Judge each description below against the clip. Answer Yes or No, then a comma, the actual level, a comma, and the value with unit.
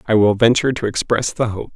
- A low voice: Yes, low, 115 Hz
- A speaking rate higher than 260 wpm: No, fast, 240 wpm